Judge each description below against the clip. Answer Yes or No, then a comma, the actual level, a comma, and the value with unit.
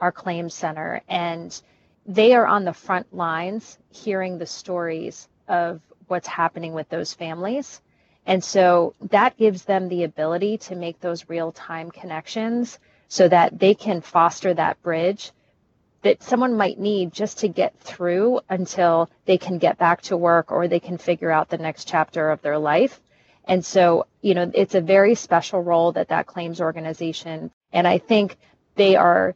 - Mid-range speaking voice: Yes, medium, 175 Hz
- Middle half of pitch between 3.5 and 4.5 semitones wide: No, narrow, 2.6 semitones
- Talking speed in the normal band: Yes, average, 170 wpm